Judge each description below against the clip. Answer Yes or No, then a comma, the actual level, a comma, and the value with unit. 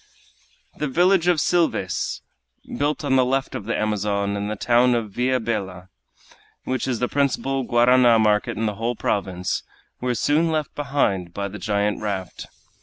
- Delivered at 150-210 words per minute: Yes, average, 165 wpm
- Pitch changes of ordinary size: Yes, average, 4.8 semitones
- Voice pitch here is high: No, low, 120 Hz